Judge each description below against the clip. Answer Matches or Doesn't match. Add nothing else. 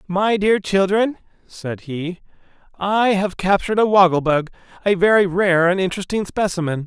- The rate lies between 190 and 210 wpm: Doesn't match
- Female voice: Doesn't match